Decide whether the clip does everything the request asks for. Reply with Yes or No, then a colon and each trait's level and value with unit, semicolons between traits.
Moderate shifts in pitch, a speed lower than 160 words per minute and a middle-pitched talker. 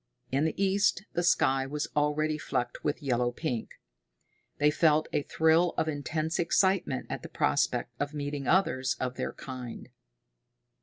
Yes: average, 3.3 semitones; average, 150 wpm; medium, 150 Hz